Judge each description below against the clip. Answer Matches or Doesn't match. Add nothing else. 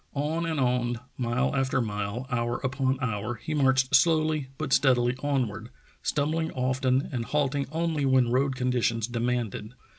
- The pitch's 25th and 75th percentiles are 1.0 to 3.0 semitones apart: Matches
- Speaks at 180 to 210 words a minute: Doesn't match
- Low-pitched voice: Matches